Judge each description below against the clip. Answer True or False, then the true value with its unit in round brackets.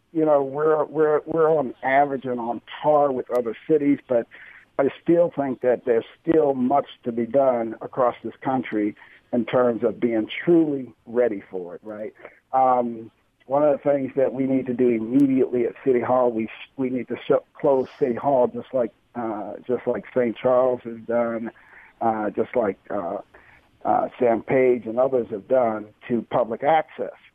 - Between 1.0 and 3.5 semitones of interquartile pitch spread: True (3.1 semitones)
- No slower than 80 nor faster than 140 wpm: False (180 wpm)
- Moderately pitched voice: False (125 Hz)